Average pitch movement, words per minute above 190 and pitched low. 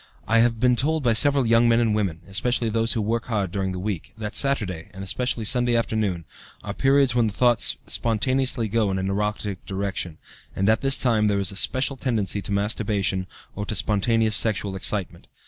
Yes: average, 3.3 semitones; average, 200 wpm; low, 110 Hz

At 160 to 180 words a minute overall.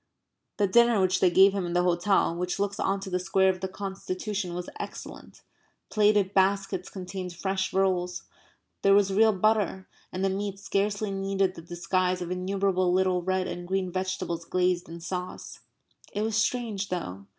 Yes: average, 175 wpm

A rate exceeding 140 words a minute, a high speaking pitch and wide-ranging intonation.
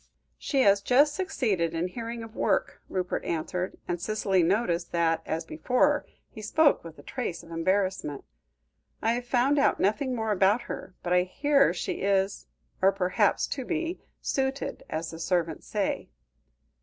Yes: average, 160 wpm; high, 200 Hz; wide, 6.7 semitones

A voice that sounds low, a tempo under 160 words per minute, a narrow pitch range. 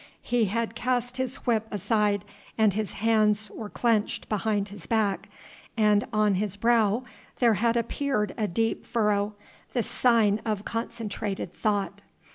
No: high, 215 Hz; average, 140 wpm; narrow, 2.0 semitones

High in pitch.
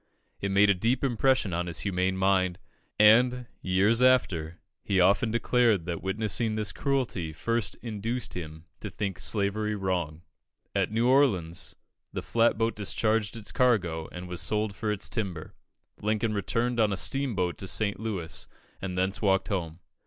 No: low, 100 Hz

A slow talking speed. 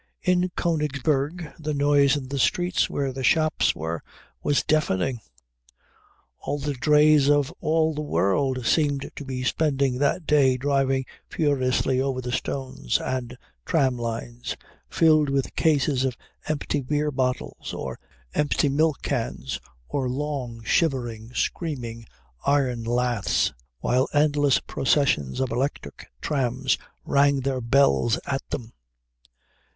Yes: slow, 125 wpm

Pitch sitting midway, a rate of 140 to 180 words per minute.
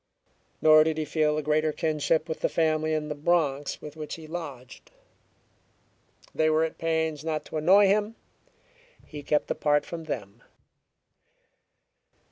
Yes: medium, 155 Hz; average, 145 wpm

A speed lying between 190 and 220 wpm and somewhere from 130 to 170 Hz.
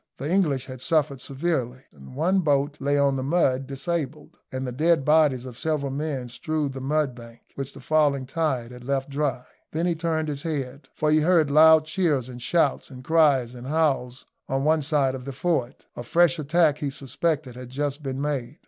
Yes: average, 195 wpm; medium, 140 Hz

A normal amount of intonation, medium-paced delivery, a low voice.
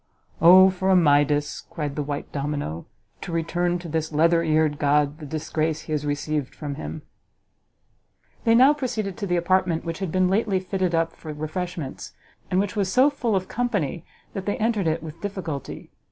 No: average, 3.9 semitones; average, 180 wpm; medium, 165 Hz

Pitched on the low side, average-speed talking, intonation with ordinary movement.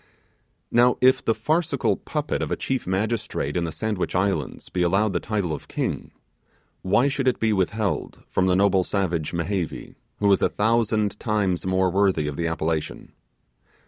Yes: very low, 95 Hz; average, 170 wpm; average, 3.7 semitones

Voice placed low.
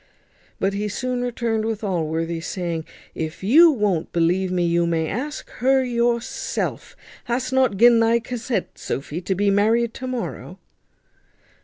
No: high, 215 Hz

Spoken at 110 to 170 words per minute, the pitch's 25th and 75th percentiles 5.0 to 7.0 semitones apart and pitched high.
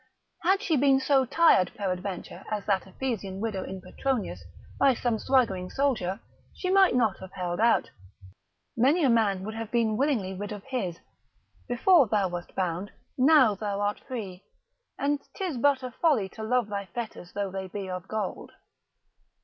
Yes: average, 165 wpm; wide, 5.5 semitones; high, 215 Hz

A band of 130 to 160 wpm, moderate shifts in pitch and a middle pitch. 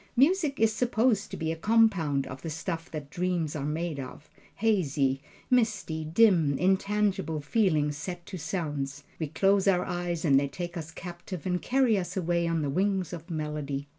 No: average, 175 wpm; average, 4.6 semitones; medium, 170 Hz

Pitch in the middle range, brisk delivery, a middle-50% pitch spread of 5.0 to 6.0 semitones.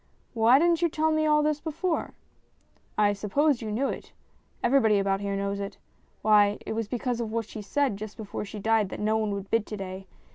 No: high, 220 Hz; fast, 230 wpm; average, 5.3 semitones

